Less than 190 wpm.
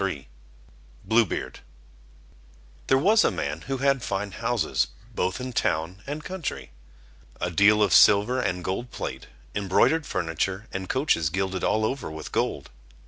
Yes: average, 150 wpm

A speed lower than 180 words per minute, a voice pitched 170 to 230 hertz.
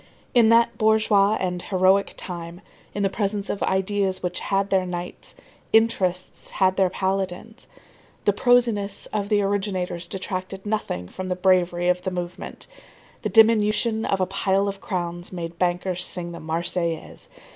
Yes: average, 150 wpm; high, 190 Hz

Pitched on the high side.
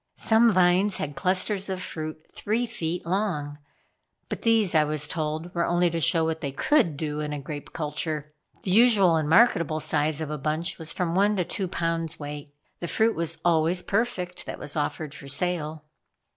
No: medium, 165 Hz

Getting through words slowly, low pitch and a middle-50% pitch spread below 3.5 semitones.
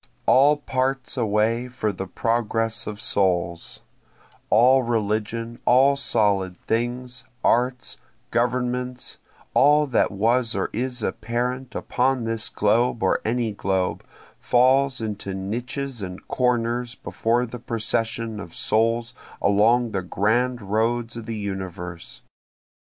Yes: slow, 115 wpm; low, 115 Hz; average, 2.9 semitones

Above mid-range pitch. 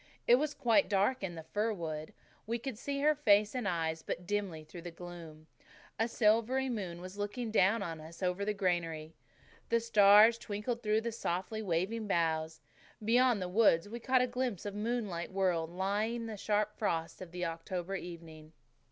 Yes: high, 200 Hz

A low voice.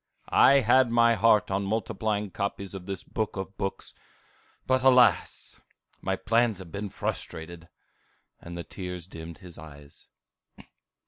Yes: low, 100 Hz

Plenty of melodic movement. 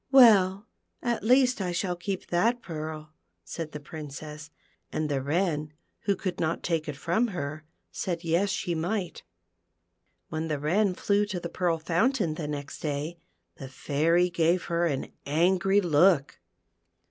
No: average, 3.9 semitones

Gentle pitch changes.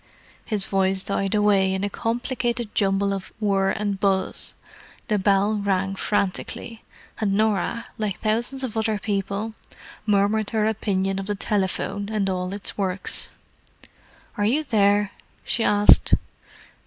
Yes: narrow, 1.9 semitones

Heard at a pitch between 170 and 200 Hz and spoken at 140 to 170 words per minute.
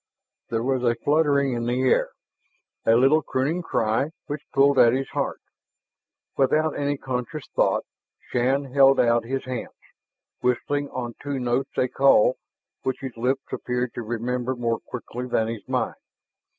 No: low, 130 Hz; average, 150 wpm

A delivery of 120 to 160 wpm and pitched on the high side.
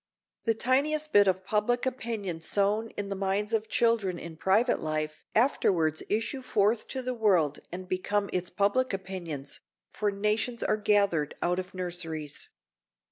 Yes: average, 150 wpm; high, 200 Hz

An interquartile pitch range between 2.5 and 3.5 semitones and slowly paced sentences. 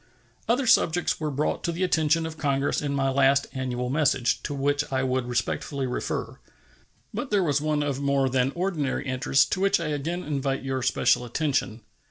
No: average, 3.0 semitones; average, 185 wpm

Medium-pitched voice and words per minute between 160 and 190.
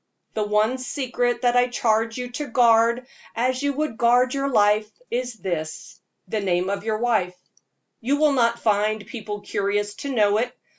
No: high, 230 Hz; average, 170 wpm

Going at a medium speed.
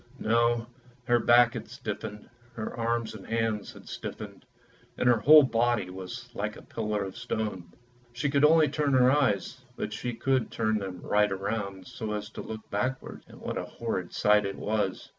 Yes: average, 180 wpm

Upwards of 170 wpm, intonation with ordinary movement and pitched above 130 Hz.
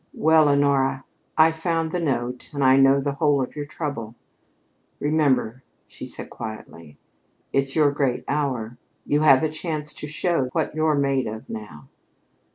No: average, 160 wpm; average, 3.2 semitones; medium, 140 Hz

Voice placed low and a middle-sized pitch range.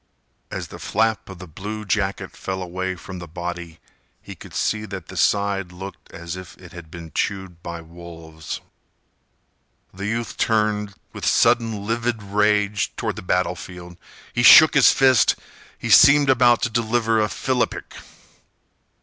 Yes: low, 100 Hz; average, 4.1 semitones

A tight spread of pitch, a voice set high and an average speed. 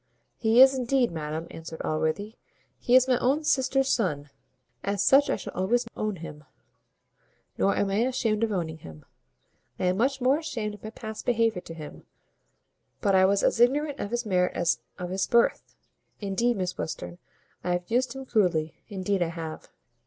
No: wide, 5.6 semitones; high, 205 Hz; average, 180 wpm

